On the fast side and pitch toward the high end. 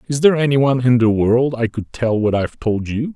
No: fast, 265 wpm; low, 125 Hz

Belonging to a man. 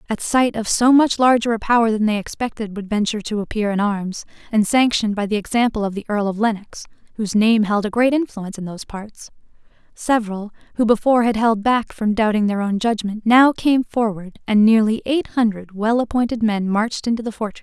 No: female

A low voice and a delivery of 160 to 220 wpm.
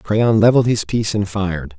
Yes: low, 105 Hz; average, 200 wpm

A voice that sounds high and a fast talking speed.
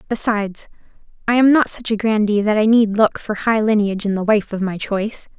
Yes: high, 215 Hz; fast, 225 wpm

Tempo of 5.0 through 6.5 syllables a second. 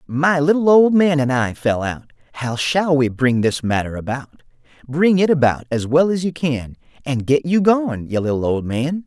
No: 4.6 syllables/s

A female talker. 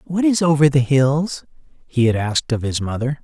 No: male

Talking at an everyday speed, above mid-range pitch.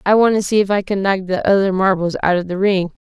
No: fast, 295 wpm; high, 195 Hz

